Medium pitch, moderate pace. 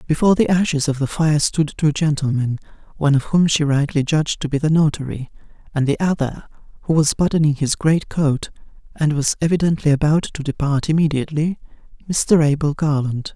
Yes: medium, 150 Hz; average, 170 wpm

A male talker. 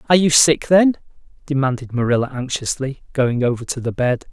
Yes: male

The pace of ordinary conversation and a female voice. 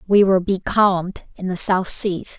Yes: average, 175 wpm; female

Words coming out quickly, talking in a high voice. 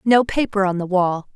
Yes: fast, 220 wpm; high, 200 Hz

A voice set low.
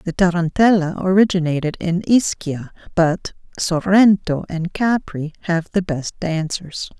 No: medium, 175 Hz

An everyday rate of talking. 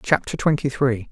Yes: average, 160 wpm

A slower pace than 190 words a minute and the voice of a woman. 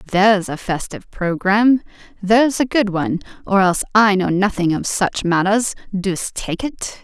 Yes: average, 160 wpm; female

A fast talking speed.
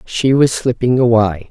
No: average, 160 wpm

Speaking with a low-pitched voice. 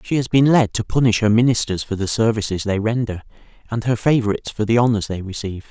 Yes: low, 110 Hz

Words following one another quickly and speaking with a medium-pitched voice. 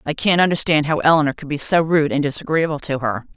Yes: fast, 230 wpm; medium, 150 Hz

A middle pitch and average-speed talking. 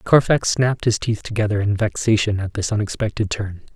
No: low, 105 Hz; average, 175 wpm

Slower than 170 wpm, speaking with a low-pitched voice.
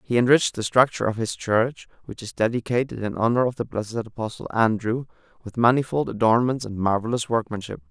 No: average, 175 wpm; low, 115 Hz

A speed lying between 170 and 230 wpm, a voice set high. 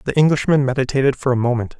No: average, 200 wpm; low, 135 Hz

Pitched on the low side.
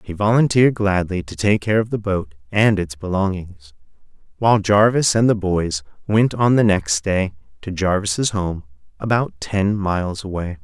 Yes: low, 100 Hz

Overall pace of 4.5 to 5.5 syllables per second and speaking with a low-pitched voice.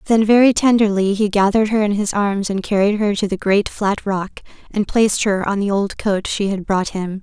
No: 5.3 syllables/s; high, 205 Hz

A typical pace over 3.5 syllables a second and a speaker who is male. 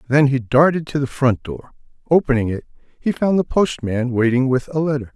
Yes: 5.4 syllables/s; male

